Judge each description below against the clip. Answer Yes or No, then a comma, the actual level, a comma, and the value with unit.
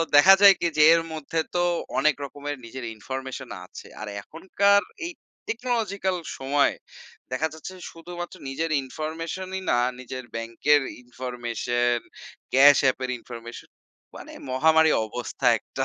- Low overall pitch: No, medium, 145 Hz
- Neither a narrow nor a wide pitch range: Yes, average, 4.7 semitones